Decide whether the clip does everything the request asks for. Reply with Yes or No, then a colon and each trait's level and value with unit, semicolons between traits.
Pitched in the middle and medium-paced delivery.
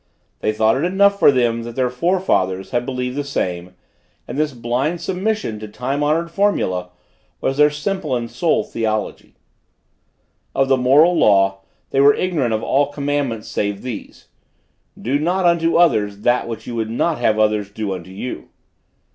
No: low, 125 Hz; average, 165 wpm